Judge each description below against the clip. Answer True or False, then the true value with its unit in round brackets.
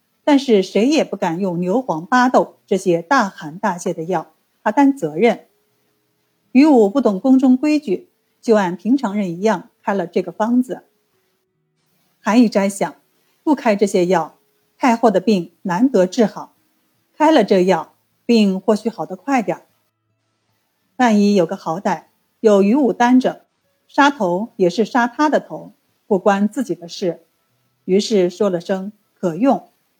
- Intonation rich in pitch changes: False (5.0 semitones)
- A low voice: False (210 Hz)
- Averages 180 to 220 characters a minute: True (210 characters per minute)